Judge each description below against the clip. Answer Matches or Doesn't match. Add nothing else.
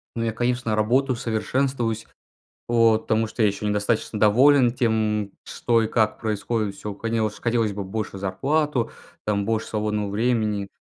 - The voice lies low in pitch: Matches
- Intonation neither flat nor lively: Doesn't match